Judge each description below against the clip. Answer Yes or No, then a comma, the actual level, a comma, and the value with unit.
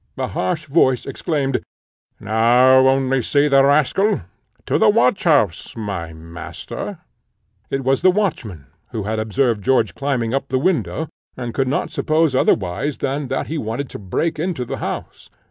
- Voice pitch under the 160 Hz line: Yes, low, 135 Hz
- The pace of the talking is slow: No, average, 160 wpm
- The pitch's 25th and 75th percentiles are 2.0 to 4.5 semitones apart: No, average, 4.9 semitones